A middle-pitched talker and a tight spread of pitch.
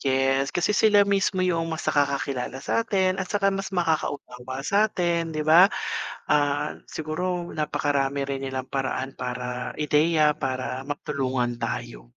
No: medium, 145 Hz; average, 4.8 semitones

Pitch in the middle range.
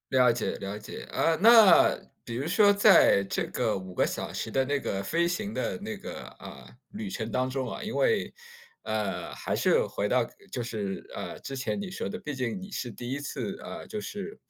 Yes: medium, 150 Hz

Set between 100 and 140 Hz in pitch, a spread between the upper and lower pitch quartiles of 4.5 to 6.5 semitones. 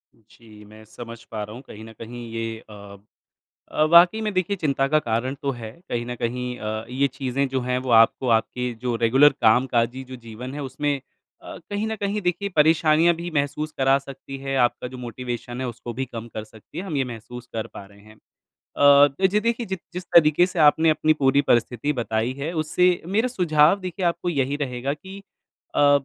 Yes: low, 135 Hz; average, 4.9 semitones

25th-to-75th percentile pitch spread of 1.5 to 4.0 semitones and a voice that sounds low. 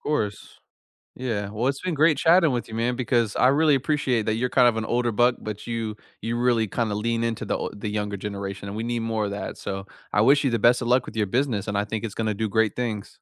Yes: average, 2.9 semitones; low, 115 Hz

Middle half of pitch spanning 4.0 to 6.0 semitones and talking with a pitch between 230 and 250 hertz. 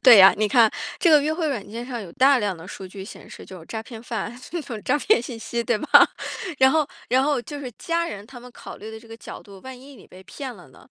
Yes: average, 4.6 semitones; high, 240 Hz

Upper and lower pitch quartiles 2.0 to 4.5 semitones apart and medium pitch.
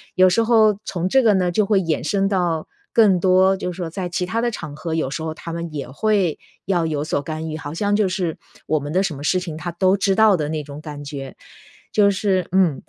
Yes: average, 3.7 semitones; medium, 180 Hz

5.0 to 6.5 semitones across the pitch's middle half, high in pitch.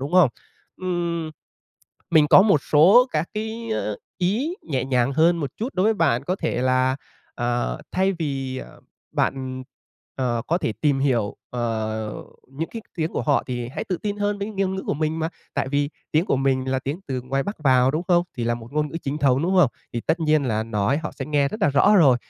No: average, 5.3 semitones; medium, 145 Hz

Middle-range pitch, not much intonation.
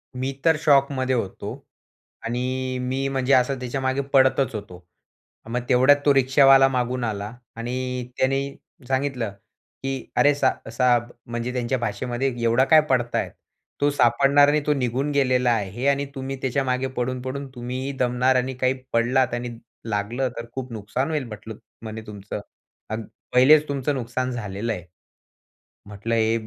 No: low, 125 Hz; narrow, 2.3 semitones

